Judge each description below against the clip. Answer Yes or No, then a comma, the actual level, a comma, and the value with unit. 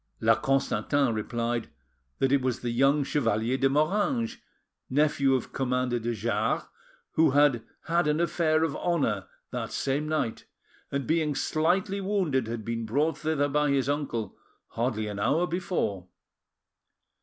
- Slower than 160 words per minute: Yes, average, 145 wpm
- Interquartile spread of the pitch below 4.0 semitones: No, average, 4.7 semitones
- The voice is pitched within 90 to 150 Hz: Yes, medium, 140 Hz